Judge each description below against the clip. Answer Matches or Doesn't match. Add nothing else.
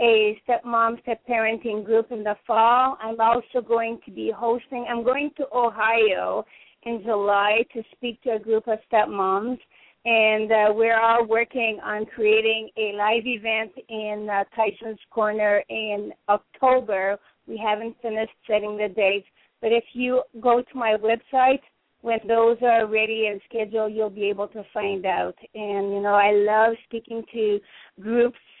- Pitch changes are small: Matches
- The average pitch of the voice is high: Matches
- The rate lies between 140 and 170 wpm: Matches